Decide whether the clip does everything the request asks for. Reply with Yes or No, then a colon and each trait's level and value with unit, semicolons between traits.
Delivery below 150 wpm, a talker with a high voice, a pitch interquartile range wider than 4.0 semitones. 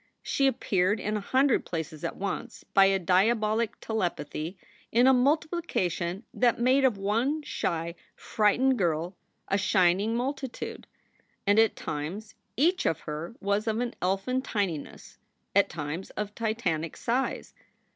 Yes: slow, 135 wpm; high, 210 Hz; average, 5.3 semitones